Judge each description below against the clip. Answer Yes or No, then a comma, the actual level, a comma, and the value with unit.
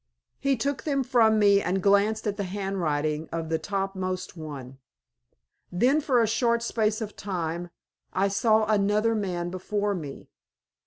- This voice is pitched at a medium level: No, high, 200 Hz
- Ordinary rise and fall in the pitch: Yes, average, 3.8 semitones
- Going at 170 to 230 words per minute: No, average, 150 wpm